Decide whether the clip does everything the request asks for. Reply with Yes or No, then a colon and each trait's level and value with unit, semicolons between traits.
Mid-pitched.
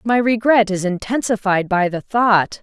No: high, 210 Hz